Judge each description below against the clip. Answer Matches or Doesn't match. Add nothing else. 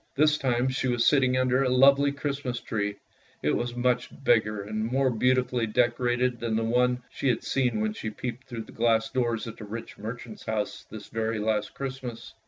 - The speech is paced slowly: Doesn't match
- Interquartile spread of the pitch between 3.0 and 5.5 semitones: Doesn't match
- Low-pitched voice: Matches